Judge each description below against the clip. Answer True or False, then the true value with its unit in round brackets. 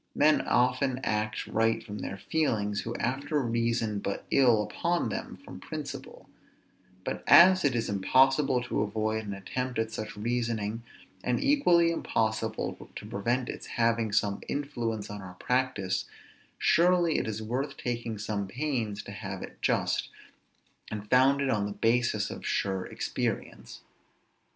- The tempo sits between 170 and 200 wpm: False (145 wpm)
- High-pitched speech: False (115 Hz)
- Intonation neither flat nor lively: True (3.9 semitones)